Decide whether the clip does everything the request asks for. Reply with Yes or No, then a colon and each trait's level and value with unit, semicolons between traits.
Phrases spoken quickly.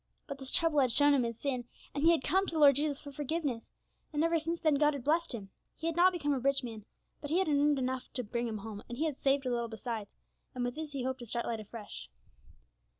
Yes: fast, 270 wpm